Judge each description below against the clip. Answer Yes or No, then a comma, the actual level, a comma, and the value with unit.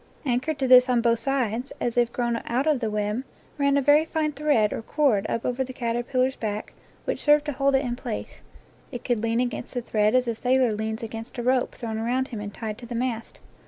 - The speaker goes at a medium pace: No, fast, 230 wpm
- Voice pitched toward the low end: No, high, 245 Hz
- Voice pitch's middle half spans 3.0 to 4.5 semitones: No, narrow, 2.6 semitones